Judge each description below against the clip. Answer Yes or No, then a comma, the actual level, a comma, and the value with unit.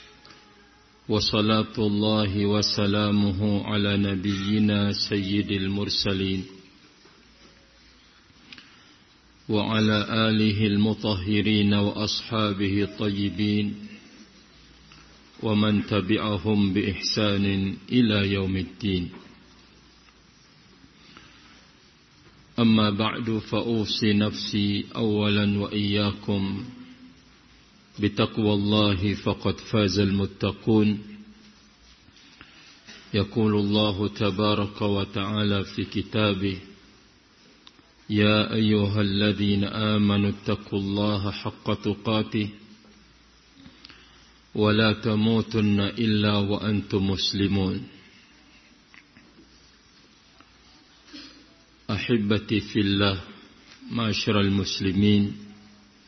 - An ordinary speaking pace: No, slow, 55 wpm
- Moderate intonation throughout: No, narrow, 1.0 semitones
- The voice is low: Yes, low, 105 Hz